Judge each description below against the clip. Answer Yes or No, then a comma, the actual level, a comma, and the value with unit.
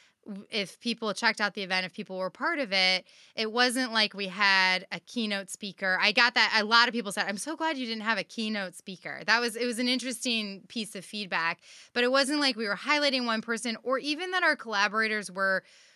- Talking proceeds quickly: Yes, fast, 230 wpm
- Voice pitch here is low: No, high, 220 Hz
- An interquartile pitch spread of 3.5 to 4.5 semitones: Yes, average, 3.8 semitones